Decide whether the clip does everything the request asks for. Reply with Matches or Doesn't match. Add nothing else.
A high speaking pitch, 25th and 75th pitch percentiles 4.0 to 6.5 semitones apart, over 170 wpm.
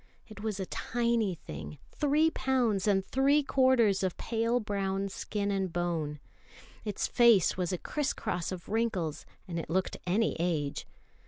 Doesn't match